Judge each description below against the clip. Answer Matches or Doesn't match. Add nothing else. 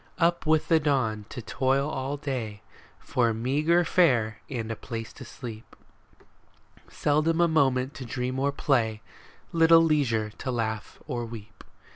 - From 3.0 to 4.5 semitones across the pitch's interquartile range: Doesn't match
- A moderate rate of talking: Matches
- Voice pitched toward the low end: Matches